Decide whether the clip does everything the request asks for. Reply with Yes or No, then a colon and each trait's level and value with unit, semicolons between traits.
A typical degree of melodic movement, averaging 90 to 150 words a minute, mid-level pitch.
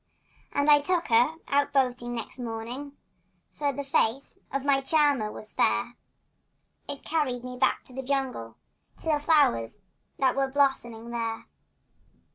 No: average, 3.2 semitones; average, 145 wpm; very high, 265 Hz